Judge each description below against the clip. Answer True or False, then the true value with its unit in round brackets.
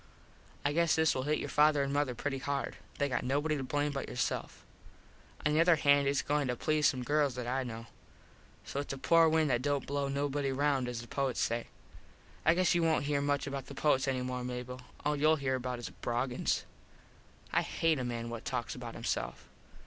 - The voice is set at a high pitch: False (140 Hz)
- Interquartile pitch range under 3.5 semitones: True (2.7 semitones)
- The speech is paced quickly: True (215 wpm)